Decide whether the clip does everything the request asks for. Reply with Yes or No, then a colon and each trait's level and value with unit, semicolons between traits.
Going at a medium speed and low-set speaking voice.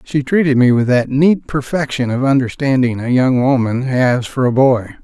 Yes: average, 190 wpm; low, 130 Hz